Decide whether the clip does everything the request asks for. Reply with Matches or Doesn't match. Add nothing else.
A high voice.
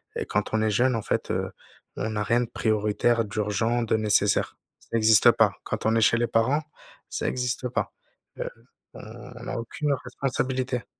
Doesn't match